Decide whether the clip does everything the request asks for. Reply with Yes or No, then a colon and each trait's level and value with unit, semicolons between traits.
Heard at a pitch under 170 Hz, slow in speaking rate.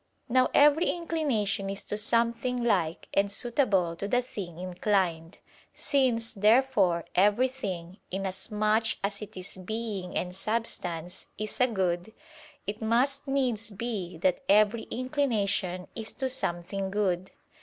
No: high, 210 Hz; slow, 125 wpm